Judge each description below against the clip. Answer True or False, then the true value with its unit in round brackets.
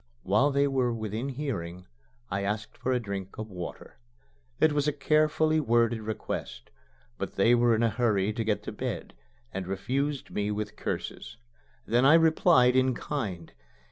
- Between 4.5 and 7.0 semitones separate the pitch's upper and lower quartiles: True (5.0 semitones)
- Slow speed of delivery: False (165 wpm)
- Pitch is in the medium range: False (115 Hz)